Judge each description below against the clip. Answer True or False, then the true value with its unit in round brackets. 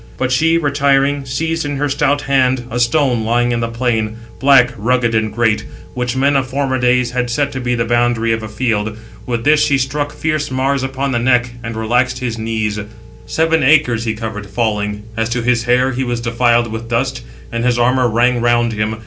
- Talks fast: True (210 wpm)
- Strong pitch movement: False (2.6 semitones)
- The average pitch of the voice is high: False (125 Hz)